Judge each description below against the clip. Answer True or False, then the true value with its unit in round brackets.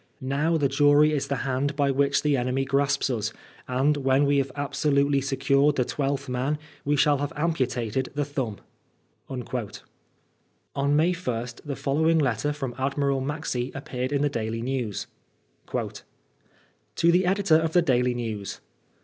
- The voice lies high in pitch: False (140 Hz)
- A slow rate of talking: False (160 wpm)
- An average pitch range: False (2.2 semitones)